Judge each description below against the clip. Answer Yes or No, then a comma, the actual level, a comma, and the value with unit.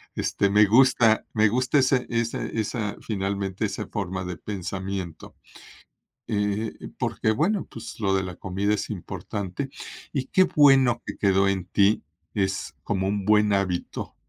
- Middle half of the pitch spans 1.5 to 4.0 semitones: Yes, average, 3.0 semitones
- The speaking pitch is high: No, low, 105 Hz